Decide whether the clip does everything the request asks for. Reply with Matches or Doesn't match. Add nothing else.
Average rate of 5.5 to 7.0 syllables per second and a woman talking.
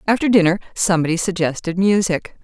Matches